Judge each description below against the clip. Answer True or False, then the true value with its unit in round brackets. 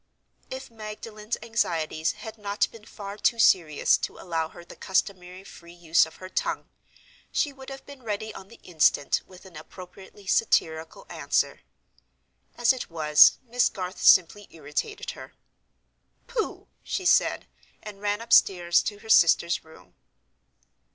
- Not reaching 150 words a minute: True (140 wpm)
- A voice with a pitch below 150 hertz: False (195 Hz)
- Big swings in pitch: False (4.7 semitones)